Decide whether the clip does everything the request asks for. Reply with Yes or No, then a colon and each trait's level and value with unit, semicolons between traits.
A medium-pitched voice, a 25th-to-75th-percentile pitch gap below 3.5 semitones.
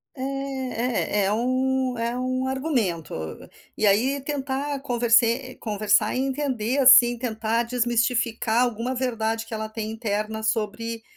No: high, 240 Hz; average, 2.8 semitones